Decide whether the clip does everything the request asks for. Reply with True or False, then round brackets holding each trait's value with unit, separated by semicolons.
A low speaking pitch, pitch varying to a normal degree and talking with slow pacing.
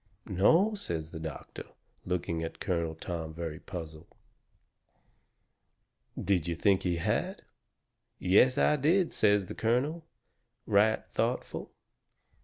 False (95 Hz; 7.1 semitones; 110 wpm)